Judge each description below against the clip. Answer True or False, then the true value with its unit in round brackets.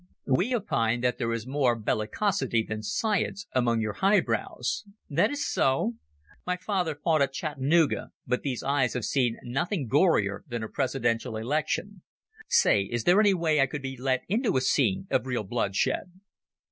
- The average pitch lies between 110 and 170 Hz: True (135 Hz)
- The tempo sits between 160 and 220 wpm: True (165 wpm)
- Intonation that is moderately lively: False (6.6 semitones)